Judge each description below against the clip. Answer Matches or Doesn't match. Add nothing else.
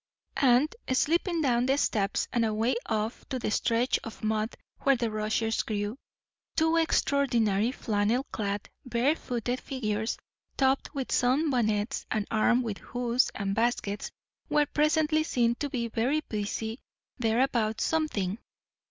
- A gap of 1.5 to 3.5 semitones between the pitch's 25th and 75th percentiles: Doesn't match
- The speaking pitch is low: Doesn't match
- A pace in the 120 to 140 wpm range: Matches